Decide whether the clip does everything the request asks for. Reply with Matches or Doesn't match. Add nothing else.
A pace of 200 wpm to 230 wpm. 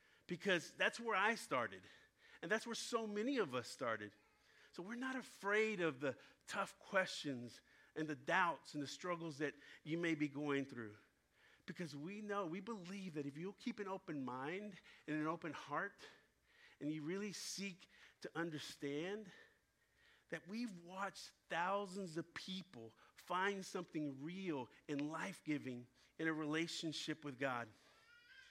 Doesn't match